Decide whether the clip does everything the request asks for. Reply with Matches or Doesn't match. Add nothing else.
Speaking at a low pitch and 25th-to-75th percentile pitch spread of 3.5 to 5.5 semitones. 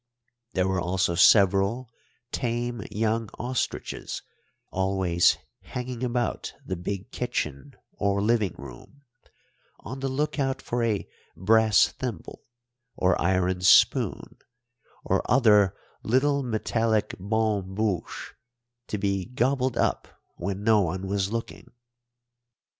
Matches